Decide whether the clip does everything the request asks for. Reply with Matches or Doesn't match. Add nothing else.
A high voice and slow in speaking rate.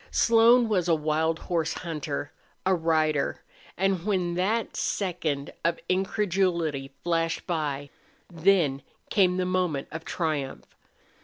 Doesn't match